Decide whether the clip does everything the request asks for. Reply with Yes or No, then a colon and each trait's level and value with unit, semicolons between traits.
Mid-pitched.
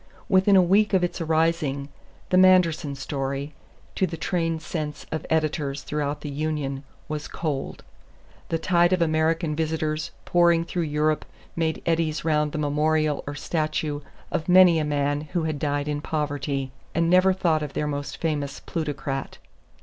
Yes: medium, 155 Hz